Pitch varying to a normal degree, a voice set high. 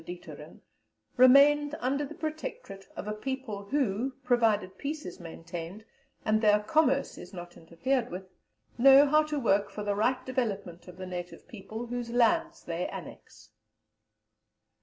No: wide, 6.0 semitones; high, 235 Hz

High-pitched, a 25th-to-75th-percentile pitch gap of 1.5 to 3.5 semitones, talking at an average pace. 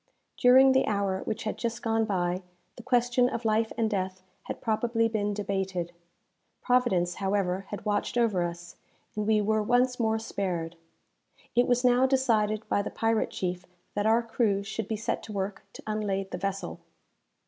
Yes: high, 215 Hz; average, 3.2 semitones; average, 170 wpm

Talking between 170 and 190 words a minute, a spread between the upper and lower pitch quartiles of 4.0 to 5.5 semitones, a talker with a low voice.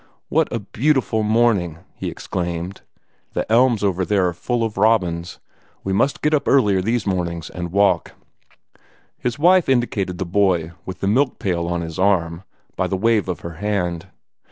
Yes: average, 180 wpm; average, 4.7 semitones; low, 100 Hz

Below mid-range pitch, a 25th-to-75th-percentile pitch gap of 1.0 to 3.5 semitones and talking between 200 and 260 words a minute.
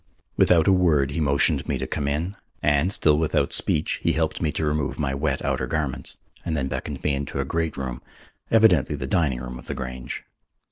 Yes: very low, 75 Hz; average, 3.0 semitones; fast, 205 wpm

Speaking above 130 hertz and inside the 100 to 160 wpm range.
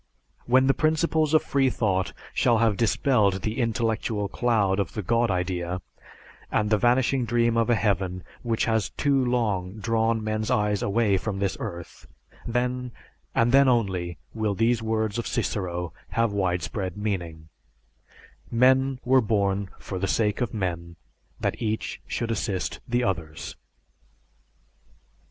No: low, 110 Hz; average, 140 wpm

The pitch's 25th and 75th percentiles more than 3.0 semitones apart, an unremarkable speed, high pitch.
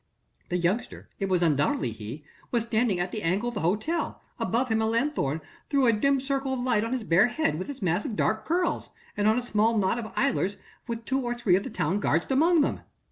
No: wide, 5.5 semitones; fast, 235 wpm; high, 220 Hz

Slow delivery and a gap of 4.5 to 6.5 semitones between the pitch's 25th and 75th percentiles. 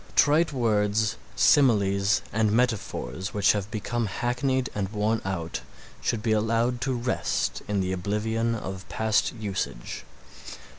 No: slow, 130 wpm; average, 3.0 semitones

